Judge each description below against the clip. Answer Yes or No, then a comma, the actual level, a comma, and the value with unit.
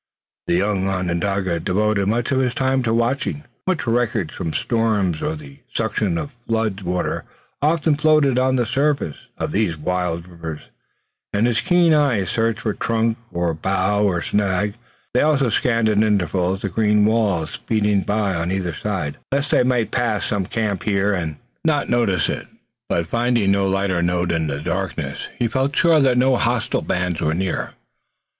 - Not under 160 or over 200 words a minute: Yes, average, 170 wpm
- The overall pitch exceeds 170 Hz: No, low, 105 Hz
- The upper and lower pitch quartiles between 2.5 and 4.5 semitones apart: No, average, 5.0 semitones